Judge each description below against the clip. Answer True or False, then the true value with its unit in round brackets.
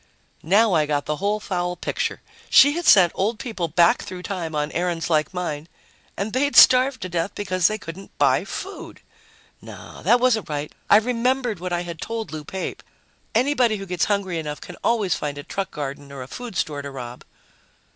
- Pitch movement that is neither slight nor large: False (5.8 semitones)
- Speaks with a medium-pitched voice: True (180 Hz)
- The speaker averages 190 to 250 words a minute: True (195 wpm)